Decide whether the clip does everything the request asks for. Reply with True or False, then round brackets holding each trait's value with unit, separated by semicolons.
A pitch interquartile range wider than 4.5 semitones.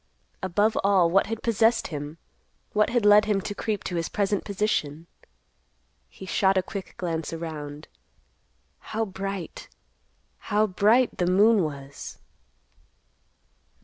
False (4.0 semitones)